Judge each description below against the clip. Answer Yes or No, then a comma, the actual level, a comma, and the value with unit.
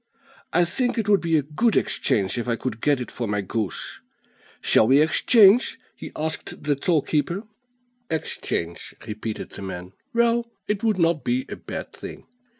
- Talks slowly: No, average, 170 wpm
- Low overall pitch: No, medium, 155 Hz